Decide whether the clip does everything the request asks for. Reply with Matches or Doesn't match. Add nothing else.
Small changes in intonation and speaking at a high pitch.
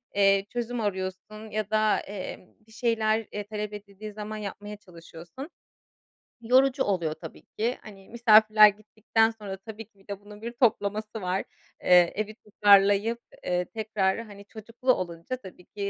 Matches